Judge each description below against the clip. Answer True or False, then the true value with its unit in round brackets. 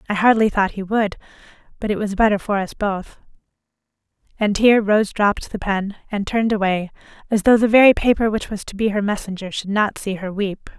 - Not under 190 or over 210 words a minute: True (205 wpm)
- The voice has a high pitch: True (205 Hz)